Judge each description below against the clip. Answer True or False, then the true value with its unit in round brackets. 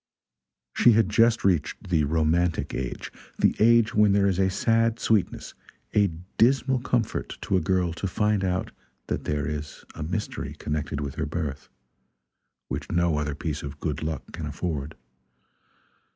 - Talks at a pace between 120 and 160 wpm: True (155 wpm)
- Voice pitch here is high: False (85 Hz)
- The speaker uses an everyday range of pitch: False (5.7 semitones)